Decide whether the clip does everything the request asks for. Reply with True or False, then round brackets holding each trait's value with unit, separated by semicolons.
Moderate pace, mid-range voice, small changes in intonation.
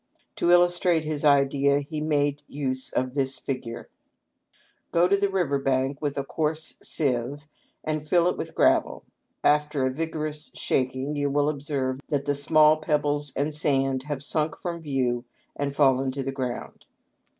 True (160 wpm; 145 Hz; 2.2 semitones)